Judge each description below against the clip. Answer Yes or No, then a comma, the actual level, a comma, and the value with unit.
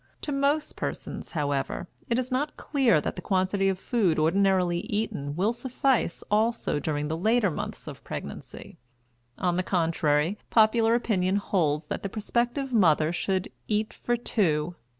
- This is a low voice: No, high, 195 Hz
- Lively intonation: Yes, wide, 6.0 semitones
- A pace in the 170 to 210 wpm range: No, average, 150 wpm